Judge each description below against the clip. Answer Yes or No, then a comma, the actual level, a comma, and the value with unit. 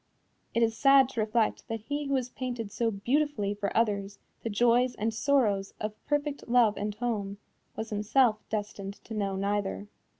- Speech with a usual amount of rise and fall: Yes, average, 3.3 semitones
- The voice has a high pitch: Yes, high, 225 Hz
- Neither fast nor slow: Yes, average, 170 wpm